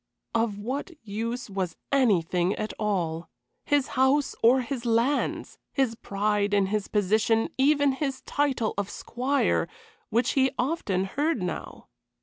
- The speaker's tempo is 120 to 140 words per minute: Yes, slow, 135 wpm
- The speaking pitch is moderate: No, high, 230 Hz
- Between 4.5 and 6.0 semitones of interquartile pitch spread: Yes, average, 4.8 semitones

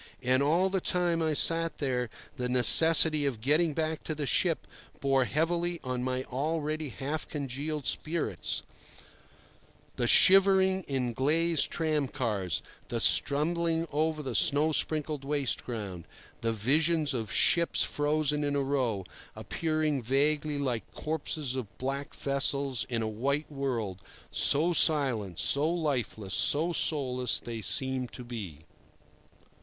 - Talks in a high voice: No, medium, 145 Hz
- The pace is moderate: No, slow, 130 wpm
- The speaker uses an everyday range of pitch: Yes, average, 3.8 semitones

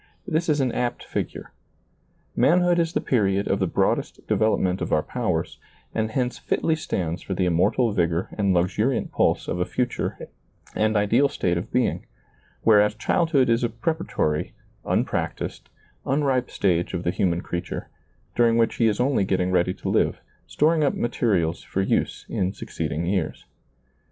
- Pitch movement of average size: No, wide, 5.8 semitones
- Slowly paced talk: No, average, 160 wpm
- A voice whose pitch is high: No, low, 110 Hz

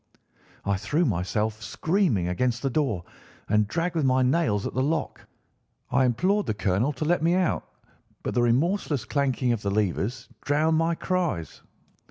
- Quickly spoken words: No, average, 165 wpm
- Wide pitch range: Yes, wide, 7.1 semitones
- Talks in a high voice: No, low, 130 Hz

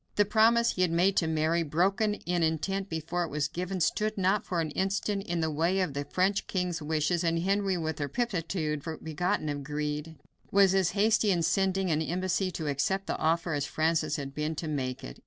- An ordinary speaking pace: No, fast, 210 wpm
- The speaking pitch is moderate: Yes, medium, 170 Hz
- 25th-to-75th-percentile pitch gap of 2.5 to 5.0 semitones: Yes, average, 3.7 semitones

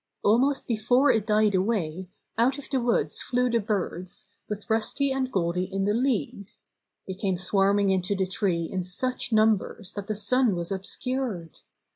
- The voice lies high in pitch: Yes, high, 210 Hz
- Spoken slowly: No, average, 165 wpm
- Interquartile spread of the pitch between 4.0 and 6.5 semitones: Yes, average, 4.3 semitones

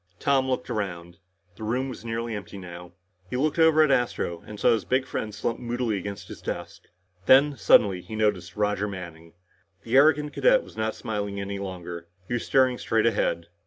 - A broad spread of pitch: No, average, 4.9 semitones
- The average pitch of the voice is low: Yes, low, 110 Hz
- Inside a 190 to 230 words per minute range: Yes, average, 195 wpm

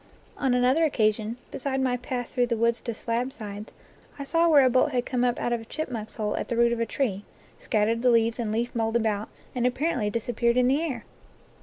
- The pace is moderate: No, fast, 230 wpm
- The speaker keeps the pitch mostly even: Yes, narrow, 2.2 semitones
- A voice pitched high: Yes, high, 240 Hz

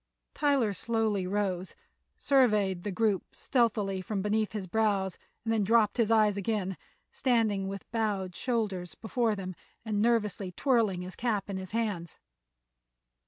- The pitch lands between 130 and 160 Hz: No, high, 210 Hz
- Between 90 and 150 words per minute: Yes, average, 140 wpm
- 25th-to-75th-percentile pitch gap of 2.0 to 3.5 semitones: Yes, average, 2.8 semitones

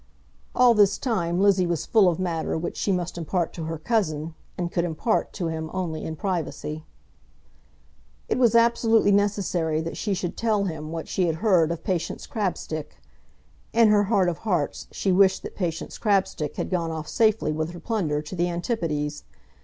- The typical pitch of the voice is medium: Yes, medium, 175 Hz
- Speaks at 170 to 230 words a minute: Yes, average, 180 wpm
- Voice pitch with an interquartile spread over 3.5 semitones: Yes, average, 4.0 semitones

